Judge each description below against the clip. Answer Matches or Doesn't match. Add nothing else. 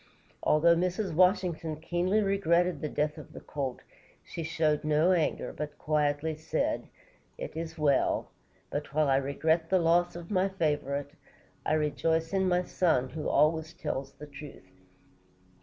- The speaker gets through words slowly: Doesn't match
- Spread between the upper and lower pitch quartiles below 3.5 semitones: Matches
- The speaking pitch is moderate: Matches